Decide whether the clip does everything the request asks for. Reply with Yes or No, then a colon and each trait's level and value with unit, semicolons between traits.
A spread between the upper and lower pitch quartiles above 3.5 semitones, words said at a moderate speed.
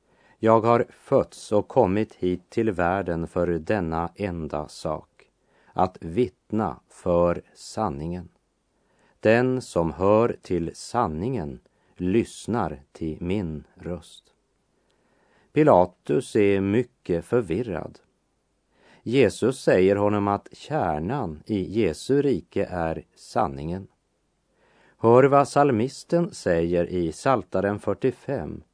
No: average, 4.7 semitones; slow, 95 wpm